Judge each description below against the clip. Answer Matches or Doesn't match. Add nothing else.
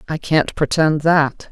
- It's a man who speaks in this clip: Doesn't match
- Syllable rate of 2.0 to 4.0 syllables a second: Matches